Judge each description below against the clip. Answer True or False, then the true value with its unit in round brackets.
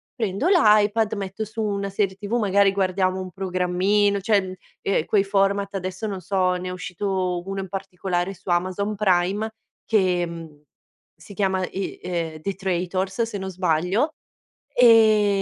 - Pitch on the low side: False (195 Hz)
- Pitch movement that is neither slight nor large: False (2.0 semitones)